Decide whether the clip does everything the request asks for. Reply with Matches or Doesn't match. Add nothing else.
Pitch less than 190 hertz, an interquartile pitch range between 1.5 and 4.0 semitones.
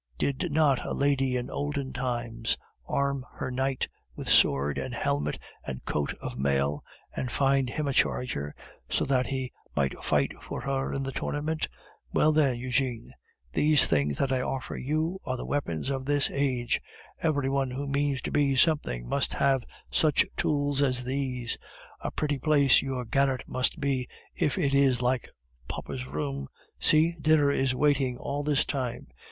Matches